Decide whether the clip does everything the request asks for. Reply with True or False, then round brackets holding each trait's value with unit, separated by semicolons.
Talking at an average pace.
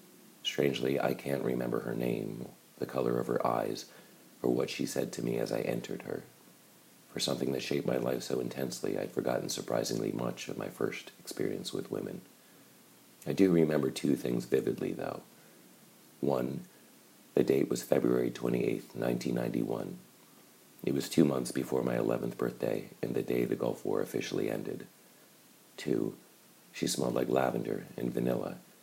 True (160 wpm)